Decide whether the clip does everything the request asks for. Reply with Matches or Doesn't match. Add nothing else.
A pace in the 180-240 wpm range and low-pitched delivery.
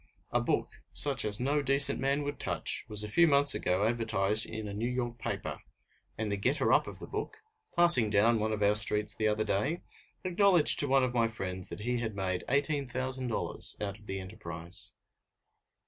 Matches